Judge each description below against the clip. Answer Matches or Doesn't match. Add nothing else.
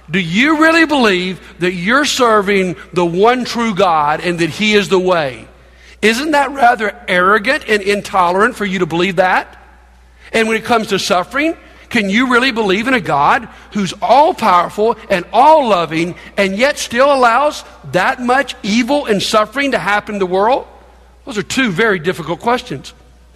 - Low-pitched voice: Doesn't match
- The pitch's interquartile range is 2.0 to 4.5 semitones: Doesn't match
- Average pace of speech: Matches